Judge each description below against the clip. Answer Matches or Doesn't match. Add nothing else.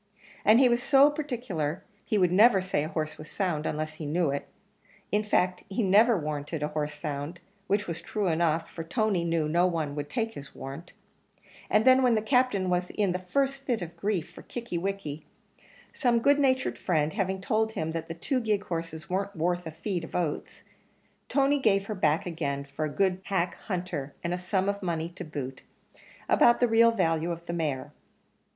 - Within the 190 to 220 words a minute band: Matches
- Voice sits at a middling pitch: Matches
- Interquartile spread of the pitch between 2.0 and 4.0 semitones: Doesn't match